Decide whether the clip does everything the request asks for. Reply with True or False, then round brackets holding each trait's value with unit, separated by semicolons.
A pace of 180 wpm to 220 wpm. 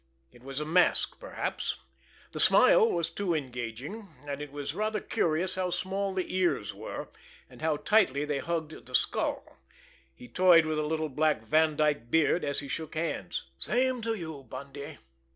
False (170 wpm)